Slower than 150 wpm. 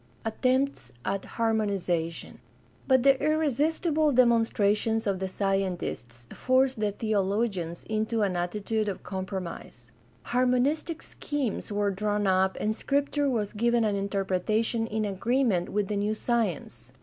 Yes: slow, 135 wpm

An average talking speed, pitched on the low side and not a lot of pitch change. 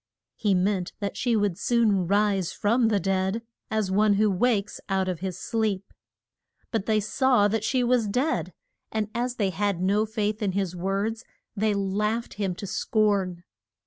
No: average, 170 wpm; high, 205 Hz; narrow, 2.3 semitones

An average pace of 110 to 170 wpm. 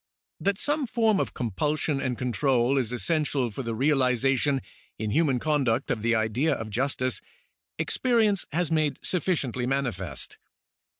Yes: slow, 135 wpm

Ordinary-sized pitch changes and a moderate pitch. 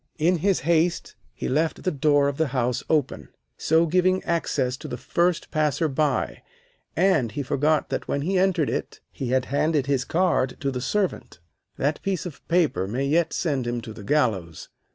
Yes: average, 4.5 semitones; medium, 150 Hz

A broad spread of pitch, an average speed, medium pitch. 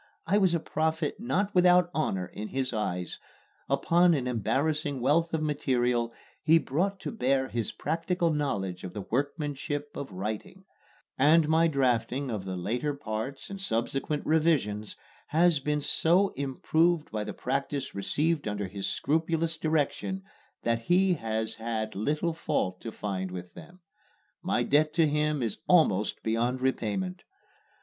Yes: wide, 6.3 semitones; average, 145 wpm; medium, 145 Hz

